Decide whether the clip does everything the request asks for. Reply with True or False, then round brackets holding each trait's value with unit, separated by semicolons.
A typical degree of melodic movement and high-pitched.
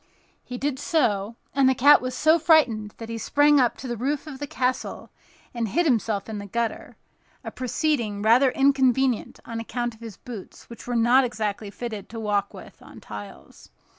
True (3.6 semitones; 240 Hz)